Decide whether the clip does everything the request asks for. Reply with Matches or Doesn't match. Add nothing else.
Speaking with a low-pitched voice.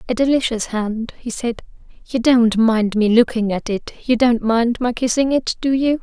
Doesn't match